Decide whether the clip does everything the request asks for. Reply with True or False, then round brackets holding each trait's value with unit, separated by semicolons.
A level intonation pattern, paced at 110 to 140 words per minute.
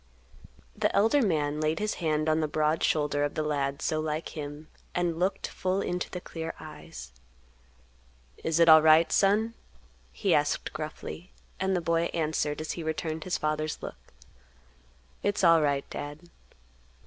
False (2.1 semitones; 150 wpm)